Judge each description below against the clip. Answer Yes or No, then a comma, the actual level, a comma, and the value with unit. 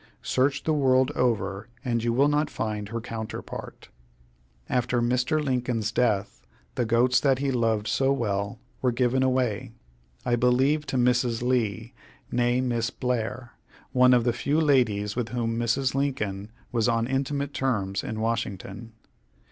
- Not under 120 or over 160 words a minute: Yes, average, 150 wpm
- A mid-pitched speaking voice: No, low, 120 Hz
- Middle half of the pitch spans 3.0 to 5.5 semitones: No, narrow, 2.4 semitones